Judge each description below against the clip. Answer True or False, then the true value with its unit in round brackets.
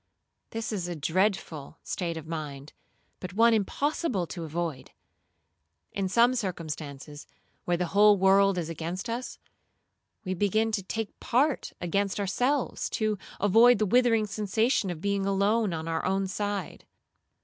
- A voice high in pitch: True (195 Hz)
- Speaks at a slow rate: False (145 wpm)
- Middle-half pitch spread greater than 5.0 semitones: False (4.1 semitones)